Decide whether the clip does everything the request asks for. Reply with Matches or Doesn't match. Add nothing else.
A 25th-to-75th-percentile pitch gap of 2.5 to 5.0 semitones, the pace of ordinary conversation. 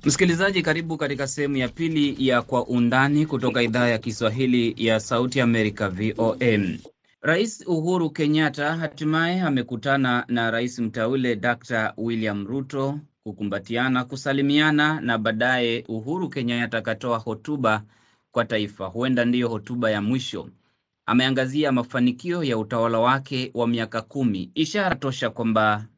Matches